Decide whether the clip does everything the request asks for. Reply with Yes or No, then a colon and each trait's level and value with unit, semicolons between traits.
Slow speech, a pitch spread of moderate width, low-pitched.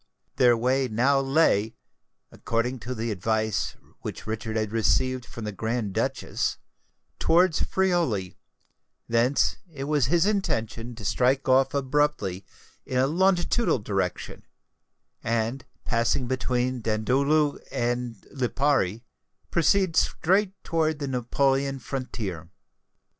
Yes: slow, 110 wpm; average, 4.1 semitones; low, 125 Hz